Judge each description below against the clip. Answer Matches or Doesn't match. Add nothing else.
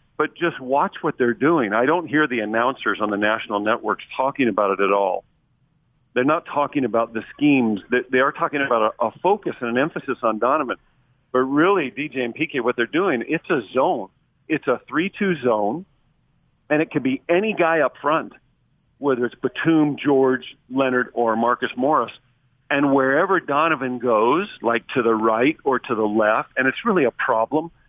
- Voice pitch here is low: Matches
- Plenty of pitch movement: Doesn't match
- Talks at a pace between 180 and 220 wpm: Matches